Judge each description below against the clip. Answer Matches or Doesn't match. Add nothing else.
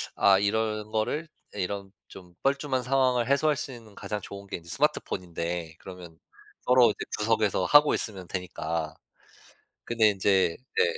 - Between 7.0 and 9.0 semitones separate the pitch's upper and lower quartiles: Doesn't match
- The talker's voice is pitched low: Matches